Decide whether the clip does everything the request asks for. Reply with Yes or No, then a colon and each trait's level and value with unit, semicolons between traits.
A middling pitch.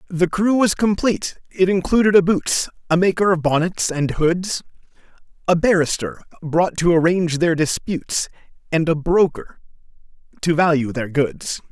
Yes: medium, 170 Hz